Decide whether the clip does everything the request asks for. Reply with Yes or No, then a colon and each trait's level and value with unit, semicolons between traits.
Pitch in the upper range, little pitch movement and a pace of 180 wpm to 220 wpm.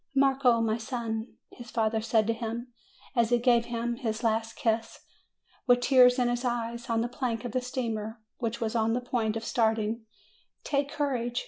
Yes: high, 235 Hz; narrow, 1.6 semitones; average, 185 wpm